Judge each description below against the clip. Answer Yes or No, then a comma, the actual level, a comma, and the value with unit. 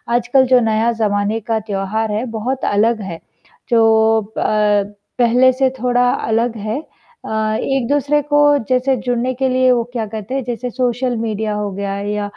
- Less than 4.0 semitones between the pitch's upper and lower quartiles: Yes, average, 2.9 semitones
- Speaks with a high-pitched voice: Yes, high, 230 Hz